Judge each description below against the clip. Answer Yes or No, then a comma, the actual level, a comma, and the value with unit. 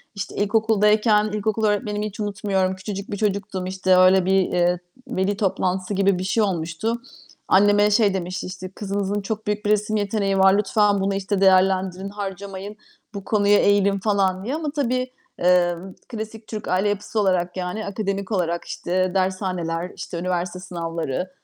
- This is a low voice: No, high, 195 Hz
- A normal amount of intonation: No, narrow, 2.1 semitones